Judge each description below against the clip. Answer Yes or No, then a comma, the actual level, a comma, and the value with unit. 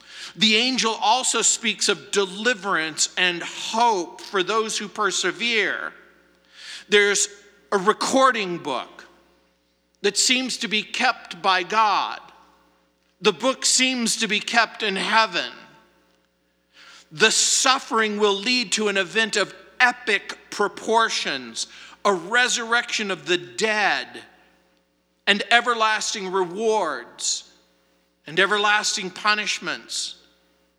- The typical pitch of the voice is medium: No, high, 210 Hz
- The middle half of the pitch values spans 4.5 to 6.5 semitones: No, average, 4.0 semitones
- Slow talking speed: Yes, slow, 100 wpm